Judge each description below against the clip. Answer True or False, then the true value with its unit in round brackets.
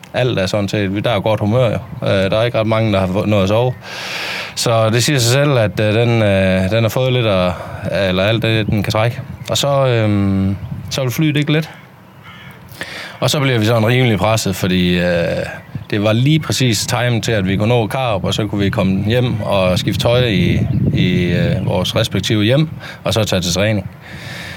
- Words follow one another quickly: False (215 wpm)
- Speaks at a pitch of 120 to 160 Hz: False (110 Hz)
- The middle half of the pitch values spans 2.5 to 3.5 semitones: False (4.0 semitones)